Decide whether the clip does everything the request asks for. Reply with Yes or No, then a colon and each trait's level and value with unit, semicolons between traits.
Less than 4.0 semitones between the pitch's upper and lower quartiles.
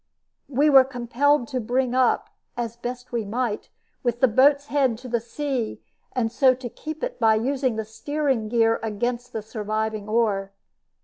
Yes: average, 2.9 semitones